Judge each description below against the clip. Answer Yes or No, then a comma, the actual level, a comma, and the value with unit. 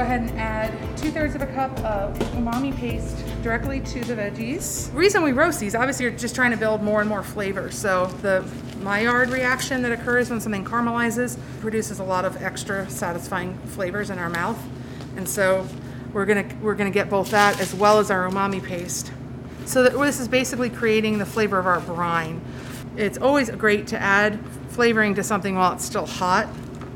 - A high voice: Yes, high, 205 Hz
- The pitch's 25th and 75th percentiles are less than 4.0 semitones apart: No, average, 4.7 semitones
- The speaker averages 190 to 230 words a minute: Yes, average, 200 wpm